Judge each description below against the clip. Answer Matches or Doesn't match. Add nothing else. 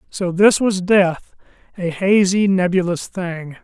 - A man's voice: Matches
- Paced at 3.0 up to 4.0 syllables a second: Matches